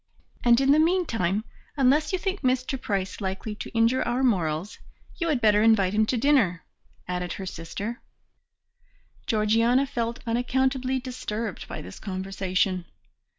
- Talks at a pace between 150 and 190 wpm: No, average, 140 wpm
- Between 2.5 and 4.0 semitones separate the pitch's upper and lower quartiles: No, average, 5.1 semitones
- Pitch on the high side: Yes, high, 230 Hz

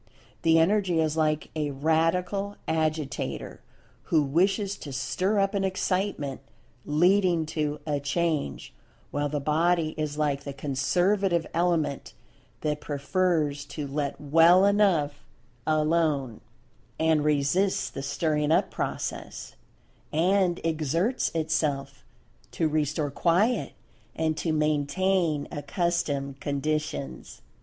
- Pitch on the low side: No, medium, 155 Hz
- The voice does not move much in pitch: No, average, 3.3 semitones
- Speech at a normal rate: No, slow, 110 wpm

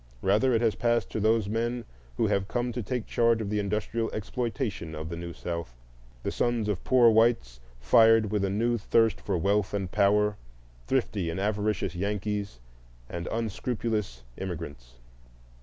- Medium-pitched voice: No, low, 105 Hz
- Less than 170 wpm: Yes, average, 155 wpm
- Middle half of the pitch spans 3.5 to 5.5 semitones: Yes, average, 4.3 semitones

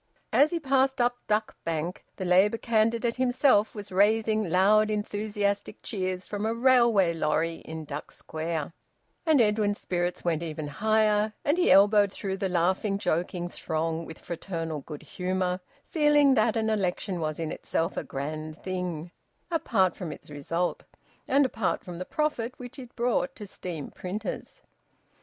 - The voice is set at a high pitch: Yes, high, 195 Hz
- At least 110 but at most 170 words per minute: Yes, average, 155 wpm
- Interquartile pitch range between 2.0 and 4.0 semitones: No, average, 4.7 semitones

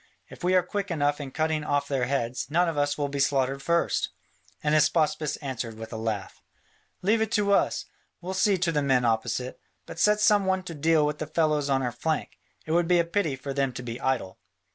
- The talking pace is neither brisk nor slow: No, fast, 225 wpm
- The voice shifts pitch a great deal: No, average, 4.3 semitones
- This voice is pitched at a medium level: Yes, medium, 150 Hz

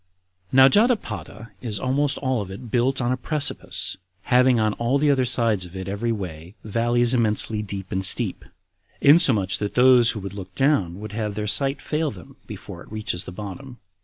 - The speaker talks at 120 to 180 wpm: No, average, 195 wpm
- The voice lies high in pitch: No, low, 115 Hz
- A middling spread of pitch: Yes, average, 4.5 semitones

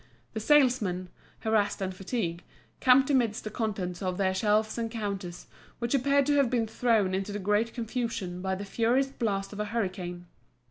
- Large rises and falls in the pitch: No, average, 3.9 semitones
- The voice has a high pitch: Yes, high, 215 Hz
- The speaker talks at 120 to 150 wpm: No, average, 175 wpm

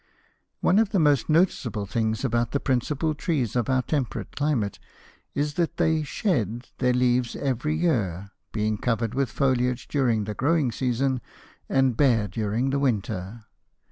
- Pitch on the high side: No, low, 125 Hz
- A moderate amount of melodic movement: Yes, average, 4.3 semitones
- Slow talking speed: No, average, 150 wpm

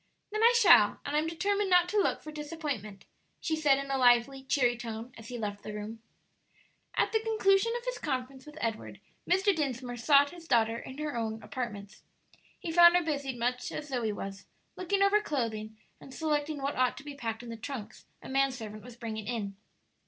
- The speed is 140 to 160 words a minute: No, average, 200 wpm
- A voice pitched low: No, very high, 270 Hz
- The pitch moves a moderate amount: No, wide, 5.7 semitones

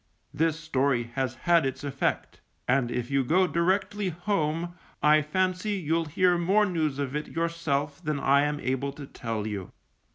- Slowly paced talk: No, average, 165 wpm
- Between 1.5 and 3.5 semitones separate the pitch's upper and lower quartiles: No, average, 4.1 semitones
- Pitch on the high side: No, medium, 150 Hz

